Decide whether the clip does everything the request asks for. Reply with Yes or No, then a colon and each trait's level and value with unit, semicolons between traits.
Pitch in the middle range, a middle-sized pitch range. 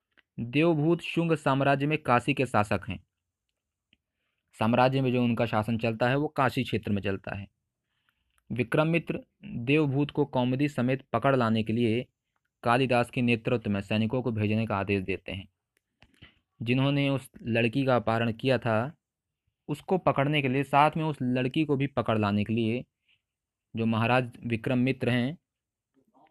No: low, 125 Hz; average, 3.8 semitones